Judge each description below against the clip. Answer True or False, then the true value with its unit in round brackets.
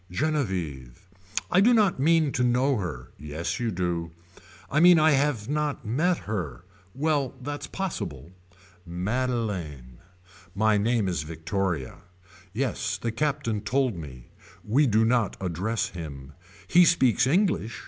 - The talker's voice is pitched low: True (110 Hz)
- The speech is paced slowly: True (130 wpm)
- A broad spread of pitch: True (8.6 semitones)